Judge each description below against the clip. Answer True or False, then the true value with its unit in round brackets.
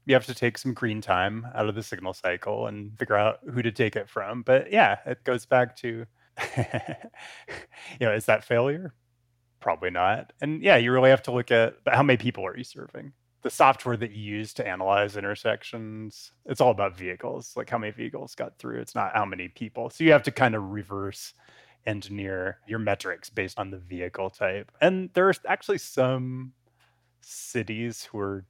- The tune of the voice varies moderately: True (3.7 semitones)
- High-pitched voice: False (115 Hz)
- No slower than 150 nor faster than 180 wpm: False (195 wpm)